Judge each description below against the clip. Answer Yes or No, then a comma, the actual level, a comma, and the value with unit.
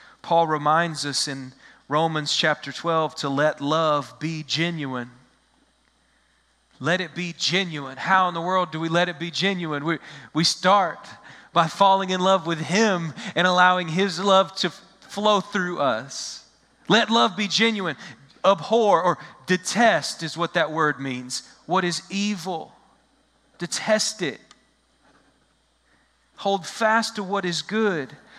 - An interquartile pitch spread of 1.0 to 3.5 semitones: No, average, 3.9 semitones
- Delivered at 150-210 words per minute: No, average, 140 wpm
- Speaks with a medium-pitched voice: Yes, medium, 175 Hz